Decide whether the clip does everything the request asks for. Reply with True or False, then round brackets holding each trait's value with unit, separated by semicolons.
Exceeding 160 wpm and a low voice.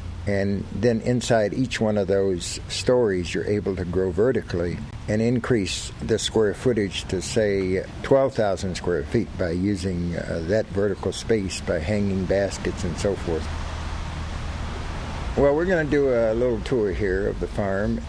False (155 wpm; 100 Hz)